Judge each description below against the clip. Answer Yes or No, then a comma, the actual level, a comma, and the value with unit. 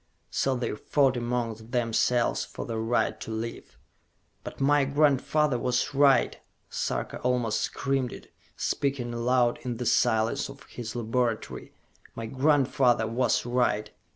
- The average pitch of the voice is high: No, low, 125 Hz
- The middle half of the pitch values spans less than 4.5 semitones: Yes, narrow, 2.6 semitones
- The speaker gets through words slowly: Yes, slow, 130 wpm